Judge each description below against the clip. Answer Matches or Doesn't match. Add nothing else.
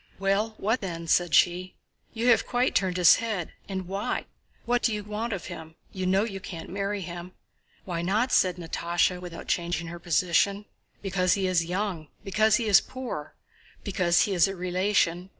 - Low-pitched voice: Doesn't match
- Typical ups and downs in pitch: Matches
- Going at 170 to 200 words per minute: Matches